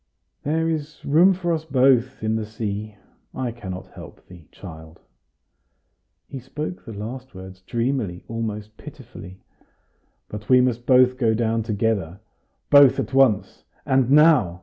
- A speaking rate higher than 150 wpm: No, average, 140 wpm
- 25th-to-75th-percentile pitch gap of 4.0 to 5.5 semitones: Yes, average, 4.4 semitones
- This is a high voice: No, low, 120 Hz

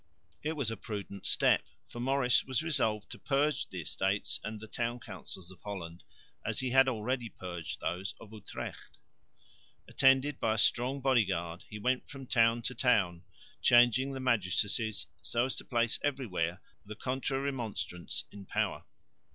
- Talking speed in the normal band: Yes, average, 160 wpm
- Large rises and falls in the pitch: No, average, 4.7 semitones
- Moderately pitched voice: No, low, 115 Hz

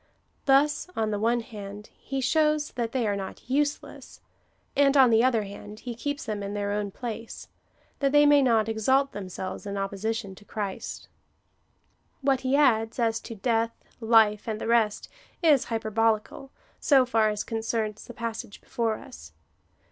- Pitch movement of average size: Yes, average, 3.7 semitones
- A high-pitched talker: Yes, high, 225 Hz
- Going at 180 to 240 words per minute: No, average, 165 wpm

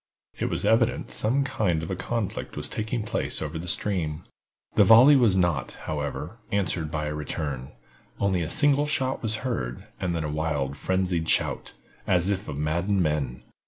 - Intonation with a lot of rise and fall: Yes, wide, 6.0 semitones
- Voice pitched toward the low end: Yes, very low, 90 Hz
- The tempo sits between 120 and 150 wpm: No, average, 175 wpm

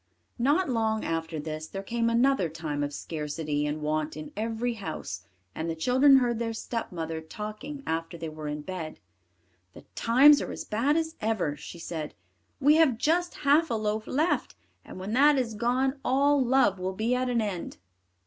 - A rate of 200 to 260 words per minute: No, average, 180 wpm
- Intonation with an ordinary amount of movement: No, wide, 8.3 semitones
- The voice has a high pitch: Yes, high, 220 Hz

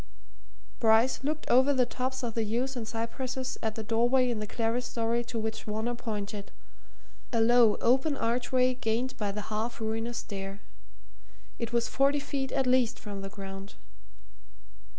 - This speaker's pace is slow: No, average, 155 wpm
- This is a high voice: Yes, high, 235 Hz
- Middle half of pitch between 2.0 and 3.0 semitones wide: Yes, narrow, 2.6 semitones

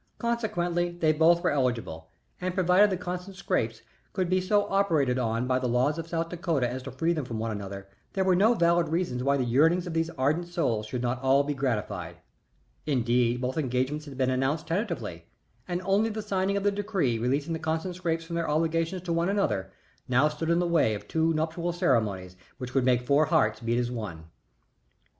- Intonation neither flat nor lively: No, wide, 5.9 semitones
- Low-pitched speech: No, medium, 155 Hz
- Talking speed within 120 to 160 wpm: No, fast, 205 wpm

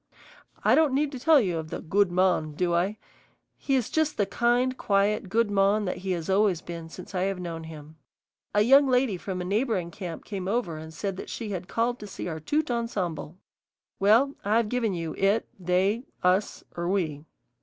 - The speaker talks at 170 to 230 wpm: Yes, average, 195 wpm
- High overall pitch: Yes, high, 195 Hz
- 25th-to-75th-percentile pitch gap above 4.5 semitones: Yes, average, 4.9 semitones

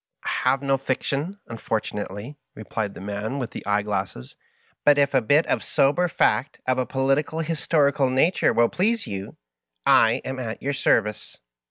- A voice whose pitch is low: Yes, low, 130 Hz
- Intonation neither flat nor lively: Yes, average, 4.9 semitones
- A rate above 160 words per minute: Yes, average, 170 wpm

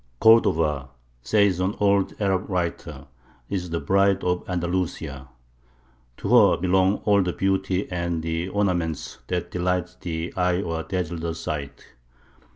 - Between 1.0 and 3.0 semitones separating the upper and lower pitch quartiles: Yes, narrow, 2.5 semitones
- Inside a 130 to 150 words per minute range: Yes, slow, 135 wpm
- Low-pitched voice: Yes, very low, 90 Hz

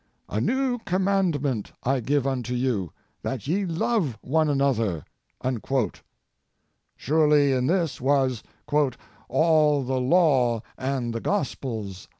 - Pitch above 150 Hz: No, low, 135 Hz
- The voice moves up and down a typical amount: Yes, average, 4.5 semitones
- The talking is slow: Yes, slow, 115 wpm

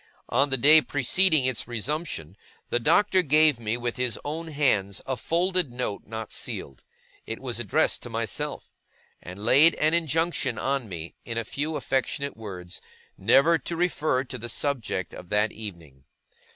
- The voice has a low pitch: Yes, low, 130 Hz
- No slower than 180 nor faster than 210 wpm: No, average, 160 wpm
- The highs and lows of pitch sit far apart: Yes, wide, 6.2 semitones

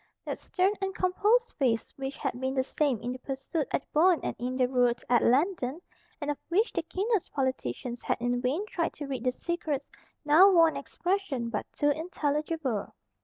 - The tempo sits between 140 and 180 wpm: No, average, 195 wpm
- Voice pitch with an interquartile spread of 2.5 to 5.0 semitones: No, wide, 5.4 semitones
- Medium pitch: No, very high, 290 Hz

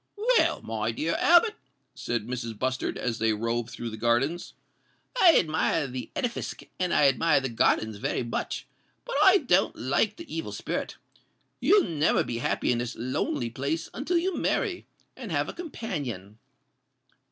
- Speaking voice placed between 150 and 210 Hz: No, low, 135 Hz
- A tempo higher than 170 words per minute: No, average, 160 wpm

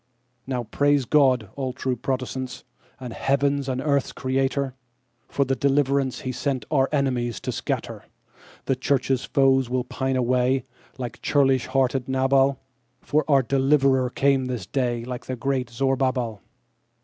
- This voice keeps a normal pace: No, slow, 130 wpm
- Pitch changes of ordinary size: No, narrow, 1.5 semitones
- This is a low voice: Yes, low, 130 Hz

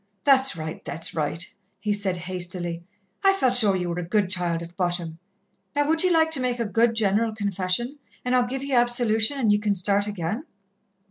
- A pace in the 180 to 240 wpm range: Yes, average, 200 wpm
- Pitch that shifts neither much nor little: No, wide, 5.8 semitones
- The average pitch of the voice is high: Yes, high, 210 Hz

